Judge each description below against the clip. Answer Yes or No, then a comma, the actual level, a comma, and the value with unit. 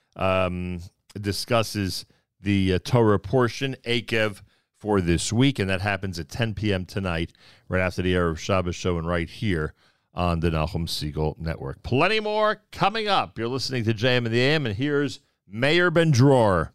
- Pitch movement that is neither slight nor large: No, wide, 6.1 semitones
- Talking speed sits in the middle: Yes, average, 170 wpm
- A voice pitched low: Yes, low, 100 Hz